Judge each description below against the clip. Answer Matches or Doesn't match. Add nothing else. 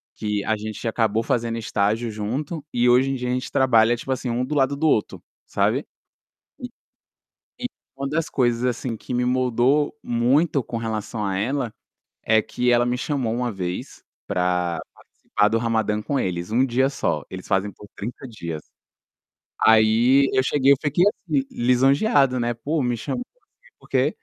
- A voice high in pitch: Doesn't match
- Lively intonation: Doesn't match